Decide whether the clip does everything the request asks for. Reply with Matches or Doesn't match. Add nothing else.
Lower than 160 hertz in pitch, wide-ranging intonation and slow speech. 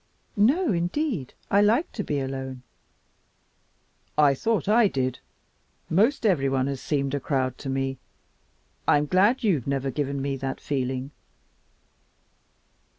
Matches